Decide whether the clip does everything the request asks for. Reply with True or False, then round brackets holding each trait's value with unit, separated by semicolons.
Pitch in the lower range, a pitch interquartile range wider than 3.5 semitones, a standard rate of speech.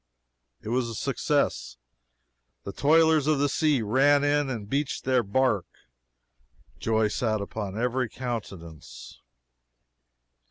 False (125 Hz; 4.9 semitones; 115 wpm)